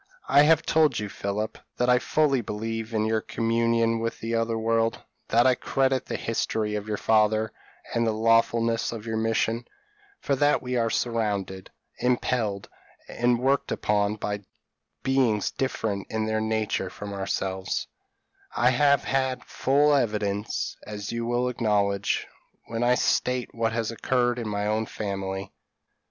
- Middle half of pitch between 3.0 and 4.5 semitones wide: No, narrow, 2.6 semitones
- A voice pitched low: Yes, low, 115 Hz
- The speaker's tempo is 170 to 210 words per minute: No, average, 150 wpm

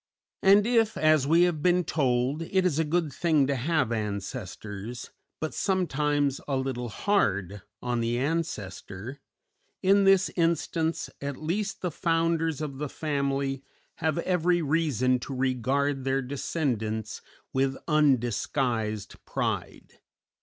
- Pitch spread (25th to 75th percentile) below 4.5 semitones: No, average, 5.0 semitones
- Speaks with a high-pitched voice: No, medium, 140 Hz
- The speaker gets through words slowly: Yes, slow, 125 wpm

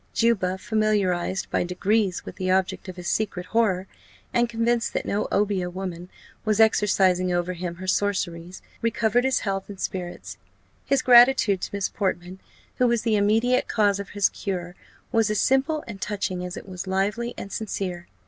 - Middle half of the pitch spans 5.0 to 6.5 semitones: No, average, 3.4 semitones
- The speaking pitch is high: Yes, high, 200 Hz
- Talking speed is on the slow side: No, average, 170 wpm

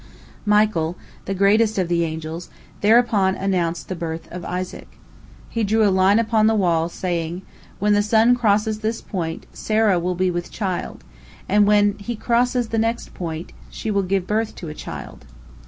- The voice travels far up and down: No, average, 3.8 semitones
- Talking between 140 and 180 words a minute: Yes, average, 170 wpm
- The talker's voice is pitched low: No, high, 195 Hz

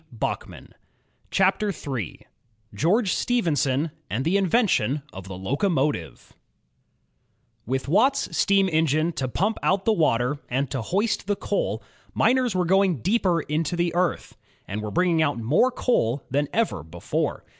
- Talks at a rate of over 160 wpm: No, average, 145 wpm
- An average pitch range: No, wide, 7.0 semitones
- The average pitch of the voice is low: No, medium, 165 Hz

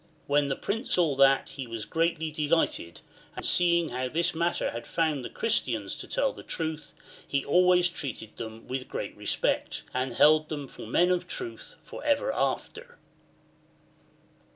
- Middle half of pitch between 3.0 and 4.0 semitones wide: No, average, 4.8 semitones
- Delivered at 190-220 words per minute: No, average, 165 wpm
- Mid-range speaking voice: Yes, medium, 155 Hz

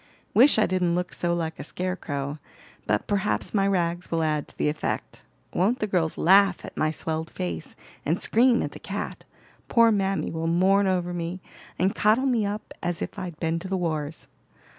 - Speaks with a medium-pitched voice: Yes, medium, 180 Hz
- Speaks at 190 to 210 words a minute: Yes, average, 195 wpm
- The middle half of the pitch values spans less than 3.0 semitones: No, average, 3.5 semitones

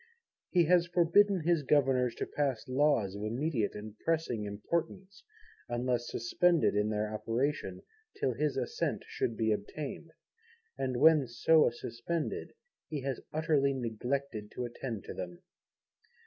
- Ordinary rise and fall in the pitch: No, wide, 6.1 semitones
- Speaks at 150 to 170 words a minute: No, slow, 135 wpm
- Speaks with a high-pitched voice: No, low, 135 Hz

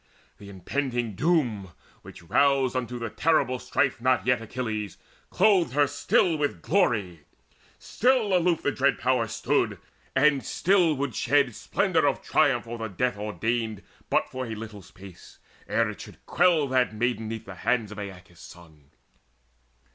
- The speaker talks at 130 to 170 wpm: Yes, average, 155 wpm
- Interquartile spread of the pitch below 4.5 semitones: No, average, 5.1 semitones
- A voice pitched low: Yes, low, 120 Hz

